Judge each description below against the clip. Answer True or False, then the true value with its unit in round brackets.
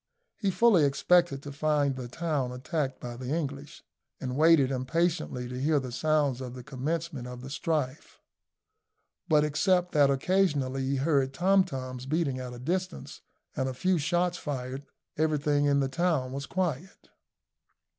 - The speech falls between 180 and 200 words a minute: False (155 wpm)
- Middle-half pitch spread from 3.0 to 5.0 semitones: True (4.0 semitones)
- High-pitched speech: False (145 Hz)